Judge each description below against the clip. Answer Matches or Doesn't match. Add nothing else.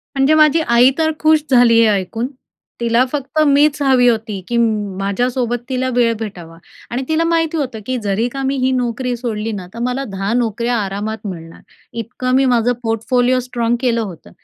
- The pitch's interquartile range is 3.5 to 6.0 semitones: Doesn't match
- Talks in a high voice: Matches